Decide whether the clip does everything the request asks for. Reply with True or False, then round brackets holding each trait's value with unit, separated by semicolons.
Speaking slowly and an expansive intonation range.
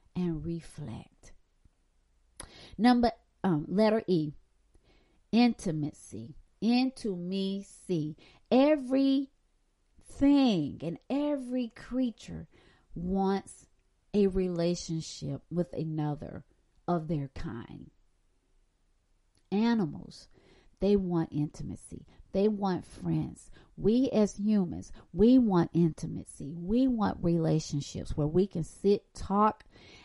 True (90 wpm; 5.9 semitones)